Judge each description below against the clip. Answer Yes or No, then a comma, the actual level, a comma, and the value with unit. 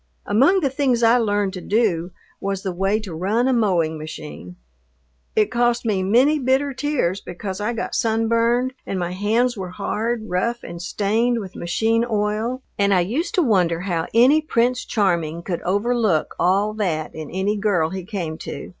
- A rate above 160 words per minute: Yes, average, 175 wpm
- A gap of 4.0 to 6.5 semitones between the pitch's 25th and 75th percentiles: Yes, average, 4.7 semitones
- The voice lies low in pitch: No, high, 210 Hz